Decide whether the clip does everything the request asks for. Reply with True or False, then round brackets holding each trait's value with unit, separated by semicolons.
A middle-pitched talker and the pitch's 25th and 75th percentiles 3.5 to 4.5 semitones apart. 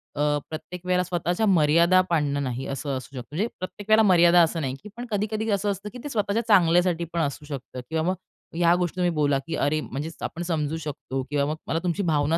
True (170 Hz; 3.8 semitones)